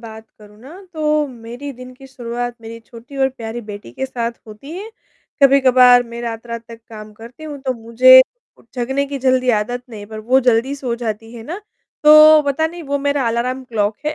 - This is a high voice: Yes, high, 245 Hz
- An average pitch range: Yes, average, 3.2 semitones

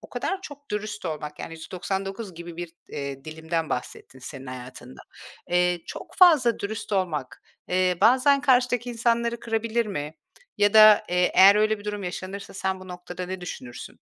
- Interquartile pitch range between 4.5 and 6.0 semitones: Yes, average, 5.1 semitones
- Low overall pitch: No, high, 190 Hz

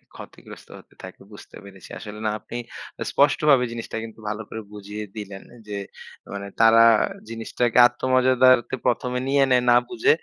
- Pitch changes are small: No, average, 3.2 semitones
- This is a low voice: Yes, low, 115 Hz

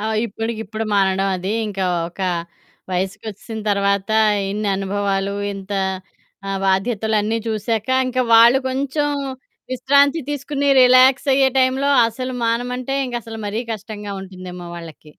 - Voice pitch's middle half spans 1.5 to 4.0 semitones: No, average, 4.6 semitones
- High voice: Yes, high, 220 Hz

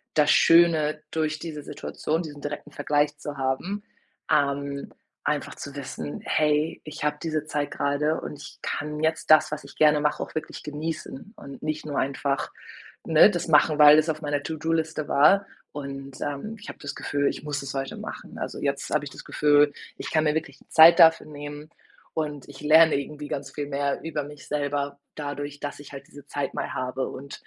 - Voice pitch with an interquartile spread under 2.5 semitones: Yes, narrow, 1.5 semitones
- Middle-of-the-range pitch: Yes, medium, 150 Hz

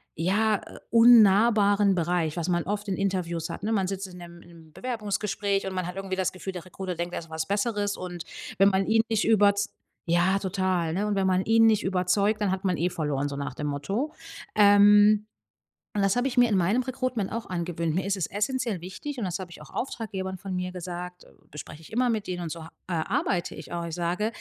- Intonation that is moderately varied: Yes, average, 3.1 semitones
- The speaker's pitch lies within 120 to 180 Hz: No, high, 190 Hz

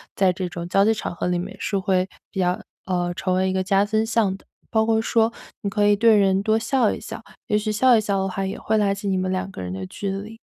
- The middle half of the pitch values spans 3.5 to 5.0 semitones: No, narrow, 2.6 semitones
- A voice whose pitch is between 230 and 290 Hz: No, high, 195 Hz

